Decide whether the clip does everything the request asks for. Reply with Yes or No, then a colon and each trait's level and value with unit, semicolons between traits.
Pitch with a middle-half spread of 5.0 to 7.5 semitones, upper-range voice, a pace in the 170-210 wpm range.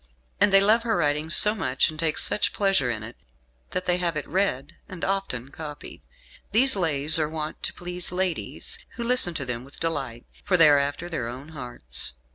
No: average, 5.3 semitones; medium, 160 Hz; average, 200 wpm